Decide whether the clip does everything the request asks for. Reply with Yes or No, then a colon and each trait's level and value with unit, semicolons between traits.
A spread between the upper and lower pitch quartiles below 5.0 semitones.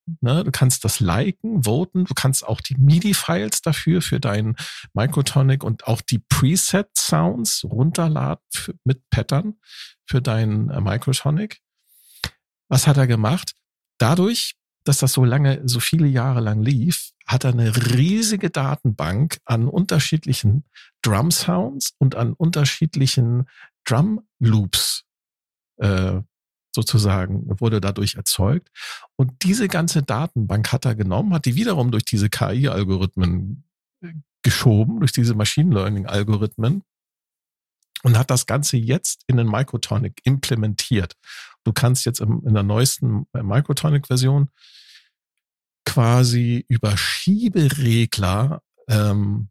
No: wide, 5.4 semitones